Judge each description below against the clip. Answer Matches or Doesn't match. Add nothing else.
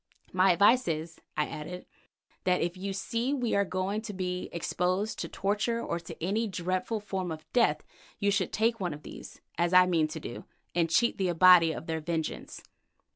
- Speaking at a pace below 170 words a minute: Doesn't match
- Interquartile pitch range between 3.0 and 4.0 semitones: Matches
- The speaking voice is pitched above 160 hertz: Matches